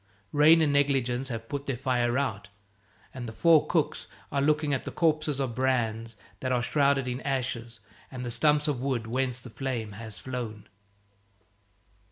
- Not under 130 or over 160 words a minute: No, average, 170 wpm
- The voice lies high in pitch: No, low, 130 Hz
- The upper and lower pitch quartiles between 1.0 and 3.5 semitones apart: Yes, average, 3.0 semitones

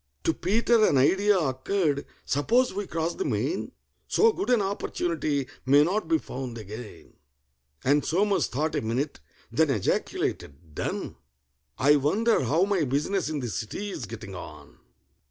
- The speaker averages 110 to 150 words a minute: Yes, average, 145 wpm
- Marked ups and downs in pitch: Yes, wide, 7.1 semitones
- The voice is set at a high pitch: No, medium, 155 Hz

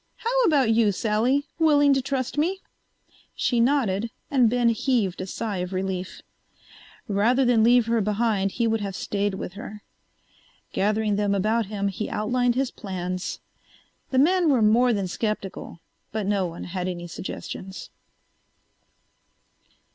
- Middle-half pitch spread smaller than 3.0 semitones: No, average, 4.1 semitones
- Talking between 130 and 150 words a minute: Yes, average, 145 wpm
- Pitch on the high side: Yes, high, 220 Hz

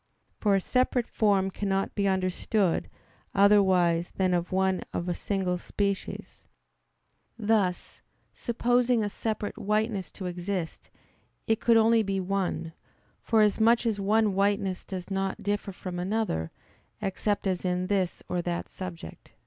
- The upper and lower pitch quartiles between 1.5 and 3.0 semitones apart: Yes, narrow, 2.6 semitones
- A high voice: Yes, high, 195 Hz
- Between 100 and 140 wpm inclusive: Yes, slow, 135 wpm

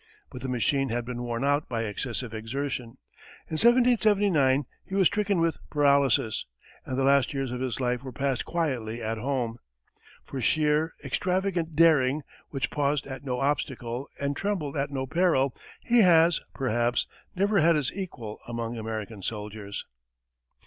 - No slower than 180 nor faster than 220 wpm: No, average, 155 wpm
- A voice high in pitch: No, low, 135 Hz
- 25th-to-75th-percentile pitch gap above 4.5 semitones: Yes, average, 4.9 semitones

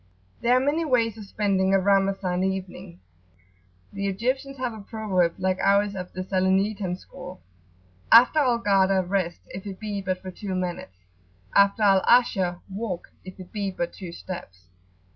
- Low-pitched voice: No, high, 195 Hz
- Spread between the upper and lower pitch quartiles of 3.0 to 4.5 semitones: No, narrow, 2.5 semitones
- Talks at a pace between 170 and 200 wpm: No, average, 160 wpm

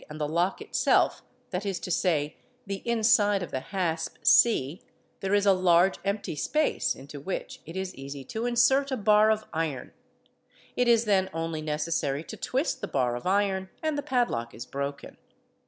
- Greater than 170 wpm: Yes, average, 180 wpm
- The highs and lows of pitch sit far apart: Yes, wide, 6.2 semitones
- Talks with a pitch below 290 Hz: Yes, high, 190 Hz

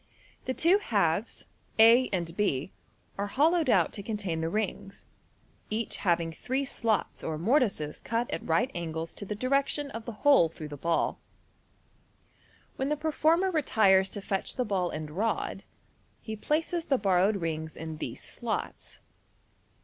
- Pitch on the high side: Yes, high, 210 Hz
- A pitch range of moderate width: No, wide, 7.5 semitones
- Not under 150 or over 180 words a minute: Yes, average, 160 wpm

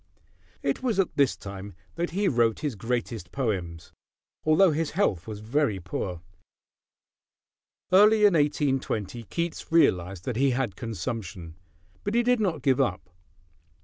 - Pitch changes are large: Yes, wide, 8.9 semitones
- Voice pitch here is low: Yes, low, 130 Hz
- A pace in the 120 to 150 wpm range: Yes, average, 140 wpm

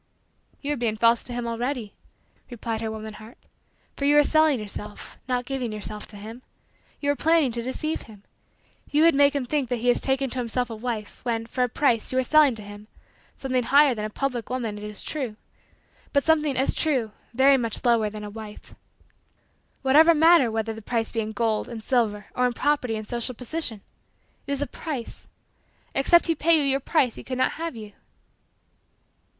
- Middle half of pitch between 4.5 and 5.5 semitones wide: No, average, 4.0 semitones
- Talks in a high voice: Yes, high, 245 Hz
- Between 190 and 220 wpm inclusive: Yes, average, 200 wpm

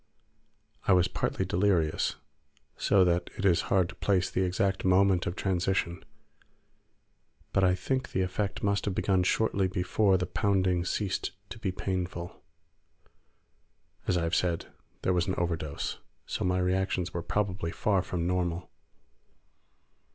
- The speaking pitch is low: Yes, very low, 90 Hz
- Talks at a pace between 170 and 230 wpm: No, average, 145 wpm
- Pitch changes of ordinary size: No, narrow, 1.6 semitones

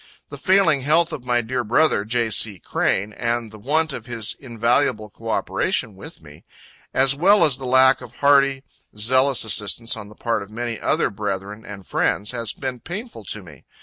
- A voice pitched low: Yes, low, 120 Hz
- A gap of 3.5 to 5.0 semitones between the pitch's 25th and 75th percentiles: Yes, average, 4.1 semitones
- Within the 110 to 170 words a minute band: No, average, 185 wpm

